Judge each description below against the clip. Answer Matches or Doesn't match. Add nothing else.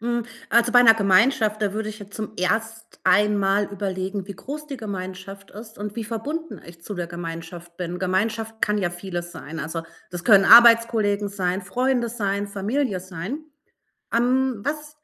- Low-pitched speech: Doesn't match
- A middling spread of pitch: Matches